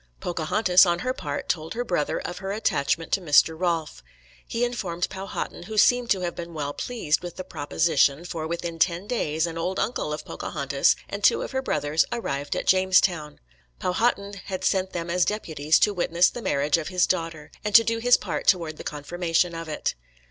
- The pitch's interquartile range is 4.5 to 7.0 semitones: No, average, 3.7 semitones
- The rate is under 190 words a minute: No, average, 195 wpm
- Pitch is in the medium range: Yes, medium, 175 Hz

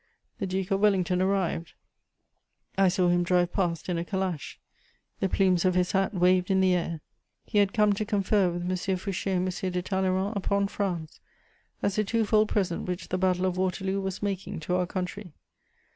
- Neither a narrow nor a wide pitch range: No, narrow, 1.6 semitones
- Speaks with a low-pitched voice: No, medium, 185 Hz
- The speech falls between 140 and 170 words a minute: No, average, 190 wpm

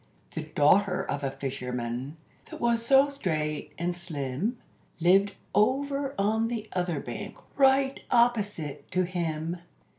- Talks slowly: Yes, slow, 125 wpm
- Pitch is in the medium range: Yes, medium, 180 Hz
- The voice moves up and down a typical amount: No, wide, 7.7 semitones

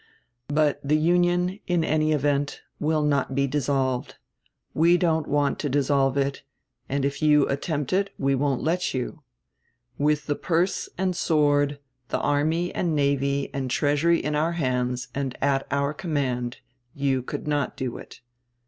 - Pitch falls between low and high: Yes, medium, 145 Hz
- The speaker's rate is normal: Yes, average, 155 wpm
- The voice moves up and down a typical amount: No, narrow, 2.3 semitones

